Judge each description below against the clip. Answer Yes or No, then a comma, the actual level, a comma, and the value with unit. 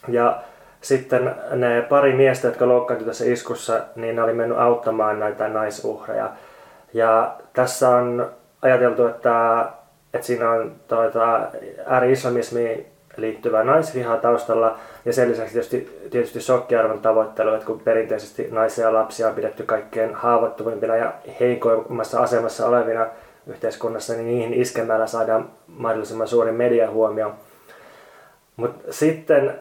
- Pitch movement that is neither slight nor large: No, narrow, 1.5 semitones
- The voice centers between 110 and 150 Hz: Yes, low, 115 Hz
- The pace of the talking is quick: No, average, 120 wpm